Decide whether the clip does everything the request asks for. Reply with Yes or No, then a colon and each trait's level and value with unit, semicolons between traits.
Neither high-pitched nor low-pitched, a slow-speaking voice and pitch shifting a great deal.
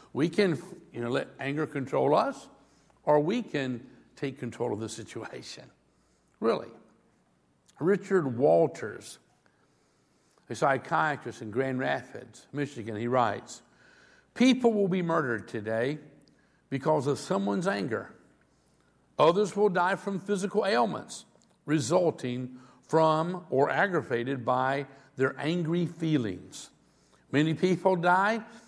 Yes: medium, 145 Hz; slow, 110 wpm; wide, 6.9 semitones